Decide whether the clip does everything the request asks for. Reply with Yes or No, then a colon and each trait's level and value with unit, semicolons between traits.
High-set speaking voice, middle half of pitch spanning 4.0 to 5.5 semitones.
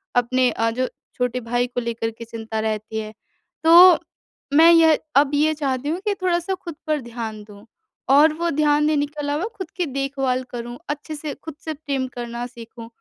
Yes: very high, 270 Hz; average, 4.6 semitones